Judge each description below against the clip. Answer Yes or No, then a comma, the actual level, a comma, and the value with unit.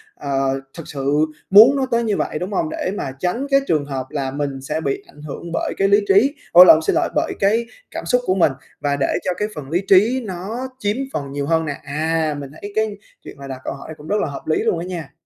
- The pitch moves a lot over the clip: Yes, wide, 6.1 semitones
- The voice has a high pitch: No, medium, 160 Hz